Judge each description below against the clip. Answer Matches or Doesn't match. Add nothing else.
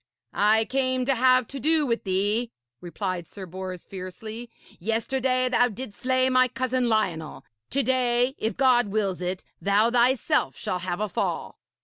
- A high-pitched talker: Matches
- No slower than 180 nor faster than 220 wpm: Doesn't match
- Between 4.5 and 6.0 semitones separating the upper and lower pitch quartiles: Matches